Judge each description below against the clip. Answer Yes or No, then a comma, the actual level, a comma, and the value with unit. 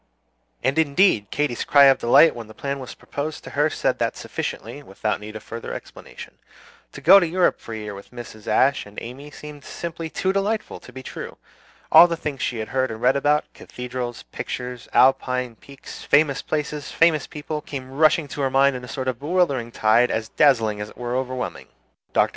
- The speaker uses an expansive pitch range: No, average, 3.8 semitones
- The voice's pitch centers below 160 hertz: Yes, low, 135 Hz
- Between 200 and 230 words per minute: Yes, fast, 205 wpm